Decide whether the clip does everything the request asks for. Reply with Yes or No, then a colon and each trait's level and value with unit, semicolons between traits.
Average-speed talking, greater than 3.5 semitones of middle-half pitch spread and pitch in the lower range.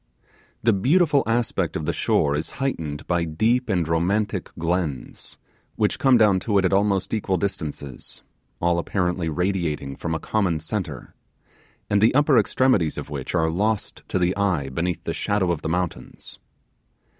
Yes: average, 160 wpm; average, 4.6 semitones; very low, 90 Hz